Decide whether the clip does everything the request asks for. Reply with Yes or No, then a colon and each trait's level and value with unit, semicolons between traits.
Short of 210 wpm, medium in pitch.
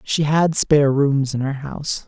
Yes: average, 200 wpm; medium, 145 Hz